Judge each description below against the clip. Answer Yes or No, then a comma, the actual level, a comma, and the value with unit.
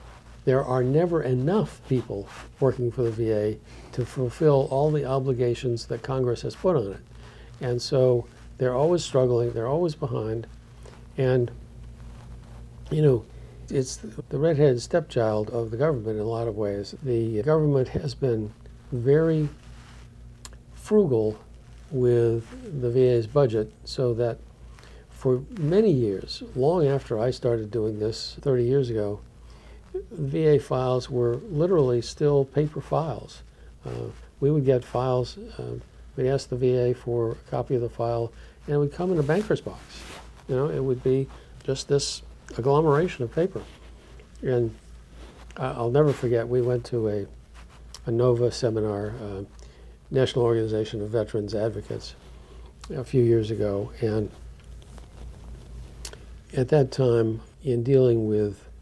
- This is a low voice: Yes, low, 120 Hz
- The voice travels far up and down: No, average, 3.9 semitones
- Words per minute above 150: No, average, 140 wpm